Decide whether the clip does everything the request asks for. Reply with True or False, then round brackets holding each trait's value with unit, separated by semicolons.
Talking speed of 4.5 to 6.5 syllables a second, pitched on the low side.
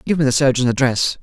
True (6.4 syllables/s; 130 Hz)